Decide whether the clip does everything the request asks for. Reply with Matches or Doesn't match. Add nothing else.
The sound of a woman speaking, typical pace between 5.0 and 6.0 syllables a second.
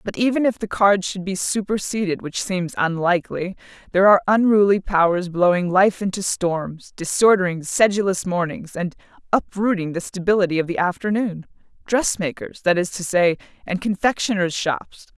Matches